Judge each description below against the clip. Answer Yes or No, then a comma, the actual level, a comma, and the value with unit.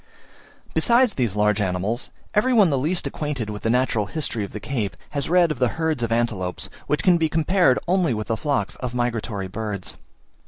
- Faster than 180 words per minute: Yes, average, 195 wpm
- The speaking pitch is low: Yes, low, 125 Hz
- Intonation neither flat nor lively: No, wide, 7.1 semitones